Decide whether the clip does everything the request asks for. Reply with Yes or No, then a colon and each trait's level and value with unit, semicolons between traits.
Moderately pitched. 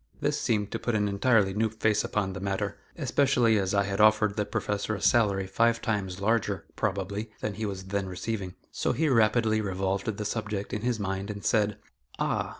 No: low, 105 Hz